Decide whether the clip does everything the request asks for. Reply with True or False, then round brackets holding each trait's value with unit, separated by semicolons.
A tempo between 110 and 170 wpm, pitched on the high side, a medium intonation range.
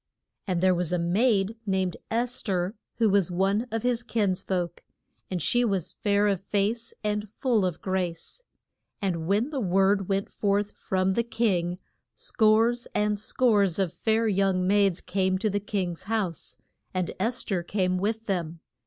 True (165 wpm; 195 Hz; 3.1 semitones)